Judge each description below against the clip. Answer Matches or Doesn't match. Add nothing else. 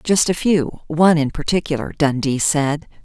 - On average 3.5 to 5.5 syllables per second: Matches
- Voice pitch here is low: Doesn't match